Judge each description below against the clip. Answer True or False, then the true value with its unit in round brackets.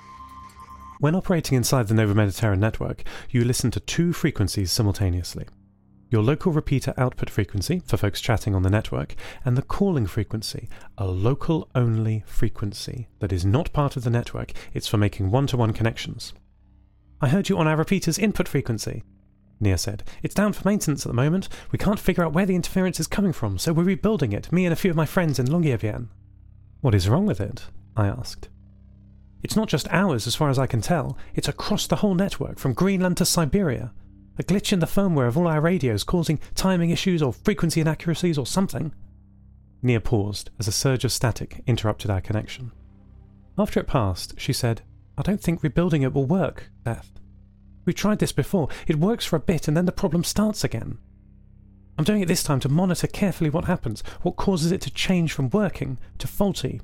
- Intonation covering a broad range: True (8.7 semitones)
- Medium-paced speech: True (195 wpm)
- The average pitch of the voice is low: True (130 Hz)